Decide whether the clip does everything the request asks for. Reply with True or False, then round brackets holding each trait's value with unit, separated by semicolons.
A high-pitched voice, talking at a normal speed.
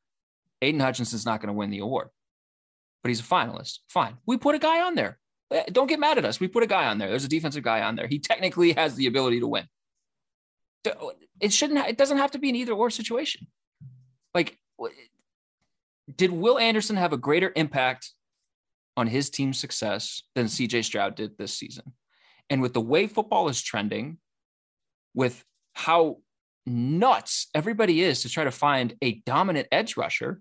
False (145 Hz; 185 wpm)